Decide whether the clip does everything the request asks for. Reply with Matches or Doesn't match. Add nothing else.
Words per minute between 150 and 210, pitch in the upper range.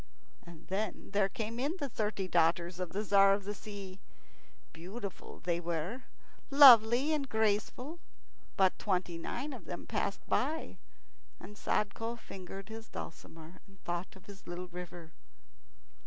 Doesn't match